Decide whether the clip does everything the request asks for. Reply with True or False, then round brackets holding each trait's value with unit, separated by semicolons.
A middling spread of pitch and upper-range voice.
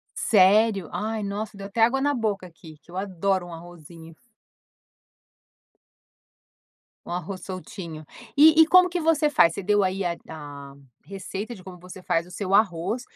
True (4.0 semitones; 195 Hz)